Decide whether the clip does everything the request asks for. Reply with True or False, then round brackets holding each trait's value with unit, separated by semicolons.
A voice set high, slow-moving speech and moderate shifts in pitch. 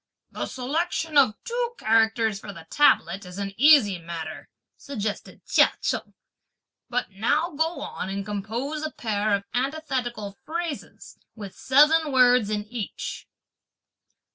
False (240 Hz; 130 wpm; 6.7 semitones)